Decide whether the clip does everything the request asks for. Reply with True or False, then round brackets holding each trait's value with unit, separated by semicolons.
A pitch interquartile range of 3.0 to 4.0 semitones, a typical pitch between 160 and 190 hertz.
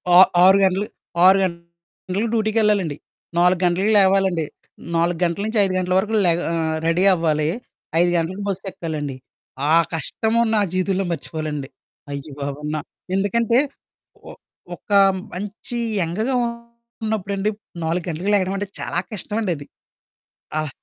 True (3.4 semitones; 185 Hz)